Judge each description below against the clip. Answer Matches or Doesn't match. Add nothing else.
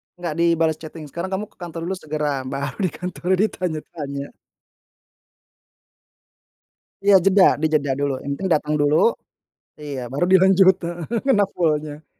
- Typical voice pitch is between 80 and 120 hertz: Doesn't match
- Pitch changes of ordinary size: Matches